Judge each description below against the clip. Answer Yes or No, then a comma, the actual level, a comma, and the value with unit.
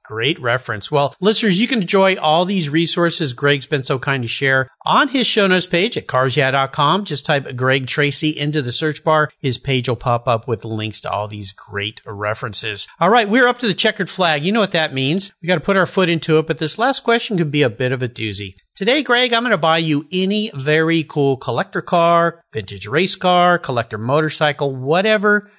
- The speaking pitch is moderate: Yes, medium, 155 Hz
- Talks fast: Yes, fast, 220 wpm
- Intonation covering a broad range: Yes, wide, 6.2 semitones